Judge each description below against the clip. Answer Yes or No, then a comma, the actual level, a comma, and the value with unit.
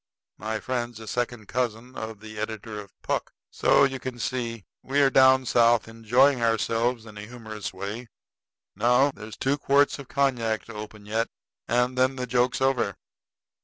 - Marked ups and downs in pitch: No, average, 2.8 semitones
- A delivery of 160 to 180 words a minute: Yes, average, 165 wpm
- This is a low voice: Yes, low, 120 Hz